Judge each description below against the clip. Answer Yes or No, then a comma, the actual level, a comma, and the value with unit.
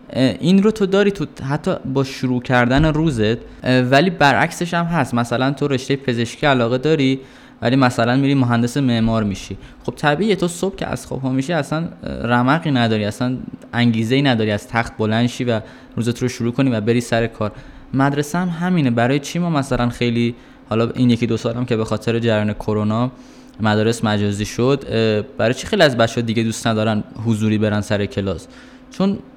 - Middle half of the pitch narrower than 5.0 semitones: Yes, average, 3.6 semitones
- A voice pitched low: Yes, low, 125 Hz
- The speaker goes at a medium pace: No, fast, 180 wpm